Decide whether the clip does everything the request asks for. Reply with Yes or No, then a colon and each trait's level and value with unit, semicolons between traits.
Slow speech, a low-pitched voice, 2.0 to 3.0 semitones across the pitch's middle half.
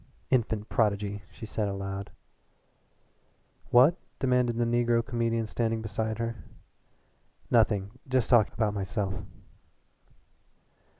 Yes: slow, 100 wpm; low, 115 Hz; narrow, 2.6 semitones